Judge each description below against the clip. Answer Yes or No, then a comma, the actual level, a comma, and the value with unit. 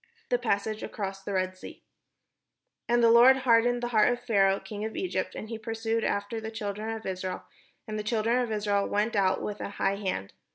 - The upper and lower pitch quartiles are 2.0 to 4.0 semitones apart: Yes, narrow, 2.4 semitones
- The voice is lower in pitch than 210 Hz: No, high, 215 Hz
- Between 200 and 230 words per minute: Yes, fast, 205 wpm